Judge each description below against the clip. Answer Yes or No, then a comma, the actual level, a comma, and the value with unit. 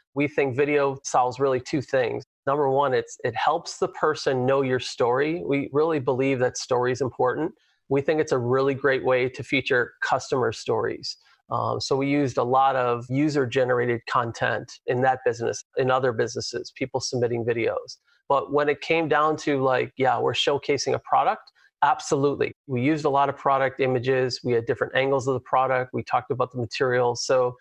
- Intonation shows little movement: Yes, narrow, 2.1 semitones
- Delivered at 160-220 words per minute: Yes, average, 190 wpm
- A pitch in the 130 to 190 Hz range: Yes, low, 135 Hz